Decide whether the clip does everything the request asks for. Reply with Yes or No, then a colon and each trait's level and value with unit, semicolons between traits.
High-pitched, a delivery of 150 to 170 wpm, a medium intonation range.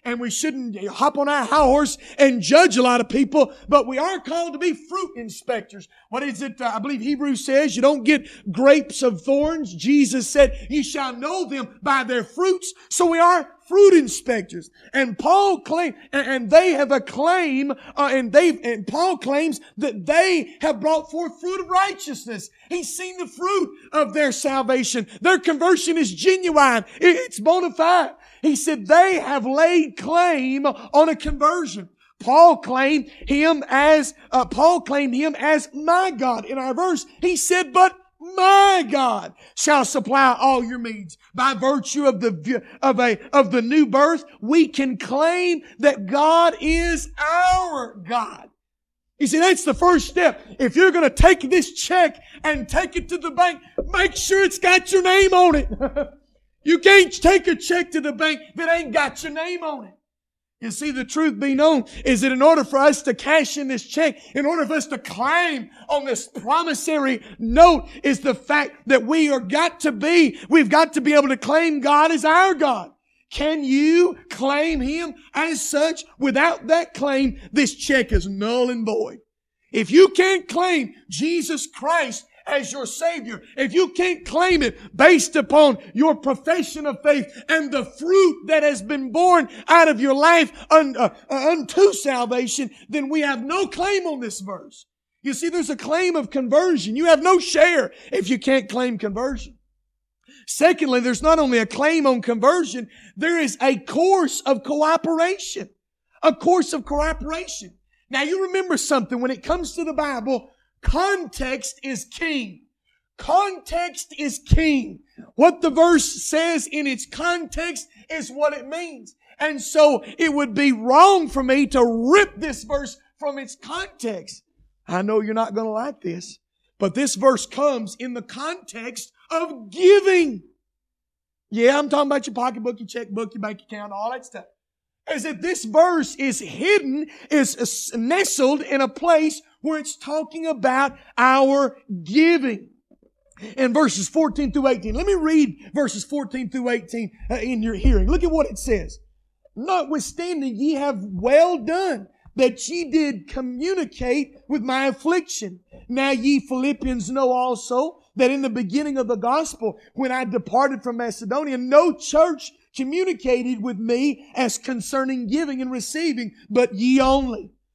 Yes: very high, 285 Hz; average, 165 wpm; average, 4.2 semitones